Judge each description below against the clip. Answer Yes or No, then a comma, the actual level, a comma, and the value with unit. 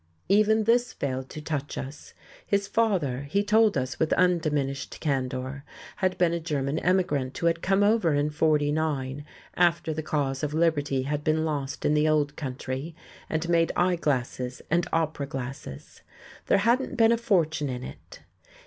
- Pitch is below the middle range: No, medium, 155 Hz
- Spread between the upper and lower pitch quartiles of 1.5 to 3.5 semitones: No, average, 4.3 semitones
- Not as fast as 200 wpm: Yes, average, 165 wpm